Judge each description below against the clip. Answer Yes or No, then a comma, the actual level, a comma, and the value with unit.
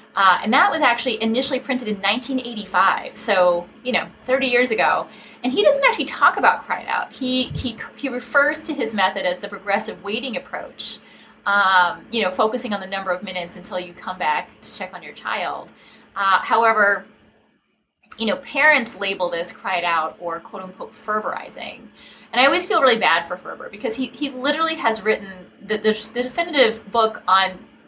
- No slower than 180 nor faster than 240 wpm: Yes, average, 185 wpm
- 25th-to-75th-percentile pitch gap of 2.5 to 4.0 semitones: No, average, 4.9 semitones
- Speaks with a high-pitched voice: Yes, high, 220 Hz